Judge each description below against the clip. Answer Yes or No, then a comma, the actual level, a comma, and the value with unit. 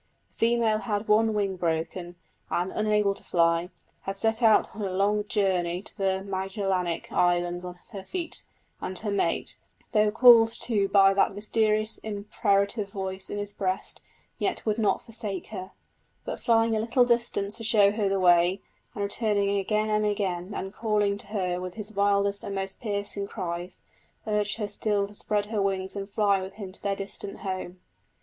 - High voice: Yes, high, 200 Hz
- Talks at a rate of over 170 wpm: Yes, average, 180 wpm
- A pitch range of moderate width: No, narrow, 2.0 semitones